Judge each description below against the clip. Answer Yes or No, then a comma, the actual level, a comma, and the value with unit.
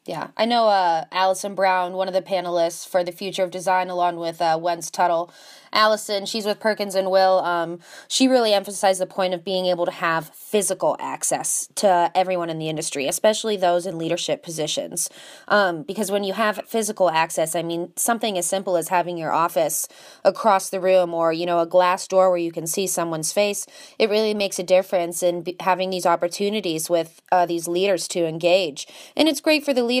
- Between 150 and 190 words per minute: No, fast, 205 wpm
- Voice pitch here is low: No, medium, 185 Hz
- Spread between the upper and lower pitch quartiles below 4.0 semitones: Yes, average, 2.8 semitones